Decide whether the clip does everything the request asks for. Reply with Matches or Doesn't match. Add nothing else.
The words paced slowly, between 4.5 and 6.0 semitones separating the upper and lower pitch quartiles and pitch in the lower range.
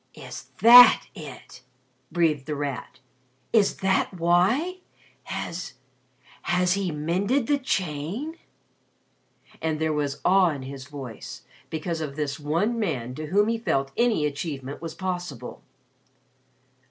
Doesn't match